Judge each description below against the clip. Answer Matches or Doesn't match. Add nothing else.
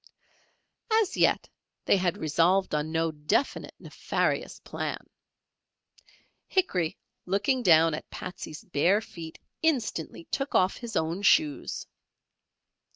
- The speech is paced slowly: Matches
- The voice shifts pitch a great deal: Matches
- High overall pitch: Doesn't match